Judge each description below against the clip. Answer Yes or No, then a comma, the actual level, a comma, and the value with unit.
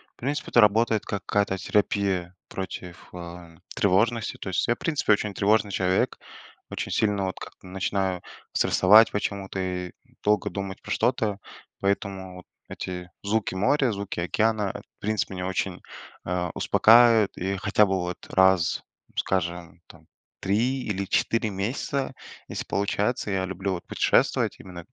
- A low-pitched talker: Yes, low, 100 Hz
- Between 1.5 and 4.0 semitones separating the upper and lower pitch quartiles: Yes, narrow, 2.6 semitones